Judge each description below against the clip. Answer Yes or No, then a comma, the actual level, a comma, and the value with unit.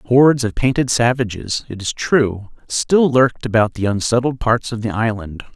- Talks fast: No, average, 175 wpm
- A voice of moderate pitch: No, low, 120 Hz